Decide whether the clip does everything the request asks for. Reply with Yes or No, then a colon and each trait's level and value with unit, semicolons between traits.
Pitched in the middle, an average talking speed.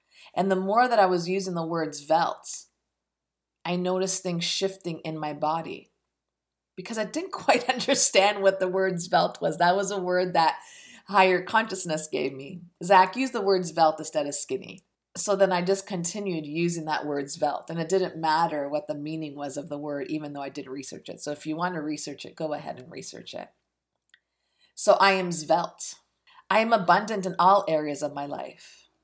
Yes: medium, 175 Hz; average, 195 wpm